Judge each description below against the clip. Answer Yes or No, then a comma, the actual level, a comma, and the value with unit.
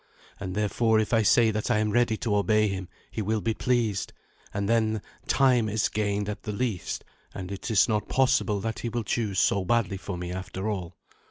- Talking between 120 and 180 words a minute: No, fast, 205 wpm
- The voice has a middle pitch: No, low, 105 Hz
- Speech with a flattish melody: Yes, narrow, 2.2 semitones